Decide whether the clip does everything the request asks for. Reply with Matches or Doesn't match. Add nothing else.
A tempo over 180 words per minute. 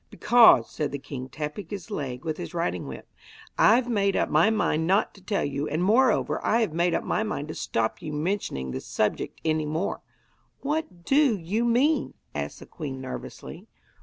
Matches